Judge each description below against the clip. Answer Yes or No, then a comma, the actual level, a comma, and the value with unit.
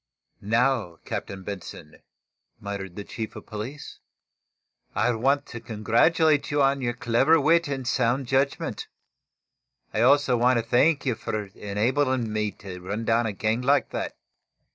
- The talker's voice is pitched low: Yes, low, 120 Hz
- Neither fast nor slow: Yes, average, 145 wpm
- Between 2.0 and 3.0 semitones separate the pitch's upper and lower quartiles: No, average, 4.2 semitones